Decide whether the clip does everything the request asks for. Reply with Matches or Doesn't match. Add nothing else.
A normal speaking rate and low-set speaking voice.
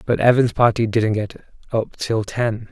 Matches